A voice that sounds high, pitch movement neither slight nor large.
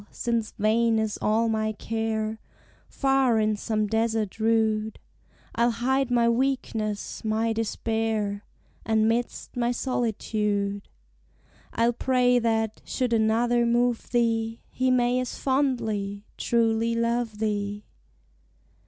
No: high, 225 Hz; narrow, 1.7 semitones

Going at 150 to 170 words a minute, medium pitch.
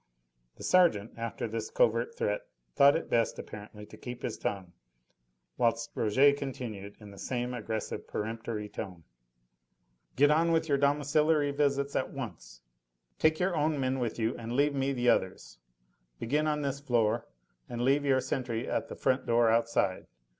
No: average, 160 wpm; low, 125 Hz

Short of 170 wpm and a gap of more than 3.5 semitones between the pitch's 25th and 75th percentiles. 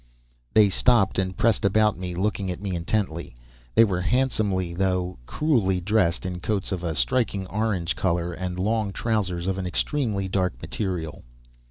No: average, 160 wpm; average, 3.0 semitones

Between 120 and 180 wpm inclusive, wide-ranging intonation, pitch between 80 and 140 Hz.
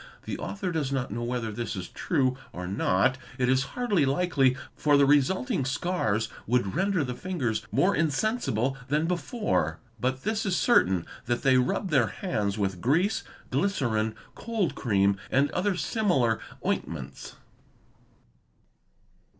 Yes: average, 140 wpm; wide, 8.1 semitones; low, 135 Hz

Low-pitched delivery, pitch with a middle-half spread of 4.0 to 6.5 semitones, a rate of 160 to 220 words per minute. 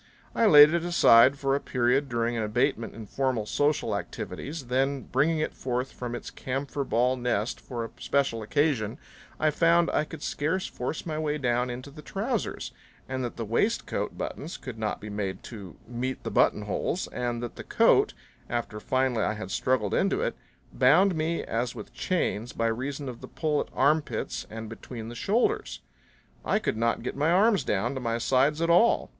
Yes: low, 130 Hz; average, 4.4 semitones; average, 185 wpm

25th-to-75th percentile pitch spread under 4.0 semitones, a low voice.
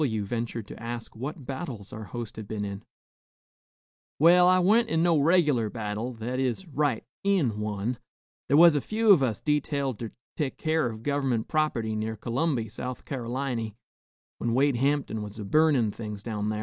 No: average, 5.2 semitones; low, 125 Hz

